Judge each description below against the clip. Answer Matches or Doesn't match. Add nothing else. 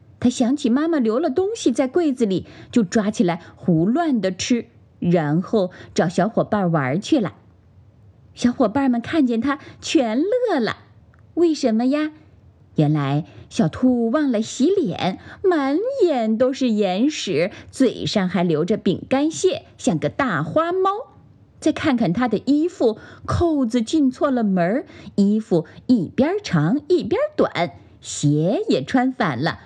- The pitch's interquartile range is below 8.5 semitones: Doesn't match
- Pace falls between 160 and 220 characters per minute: Matches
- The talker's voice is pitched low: Doesn't match